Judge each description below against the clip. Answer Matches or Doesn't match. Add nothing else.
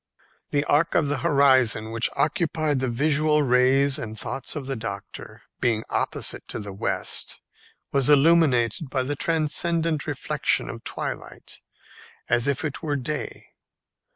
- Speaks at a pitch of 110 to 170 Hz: Matches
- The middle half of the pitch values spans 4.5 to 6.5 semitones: Doesn't match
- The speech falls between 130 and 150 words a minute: Matches